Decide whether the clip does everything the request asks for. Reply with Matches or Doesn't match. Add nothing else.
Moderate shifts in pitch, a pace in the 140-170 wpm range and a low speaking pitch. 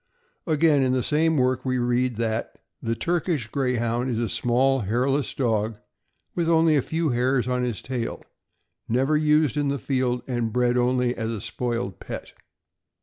Doesn't match